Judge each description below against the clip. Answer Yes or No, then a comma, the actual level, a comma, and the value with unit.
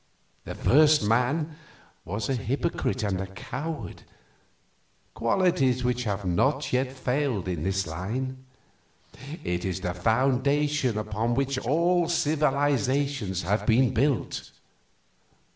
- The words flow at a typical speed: No, slow, 110 wpm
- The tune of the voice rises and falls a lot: Yes, wide, 5.7 semitones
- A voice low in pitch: Yes, low, 125 Hz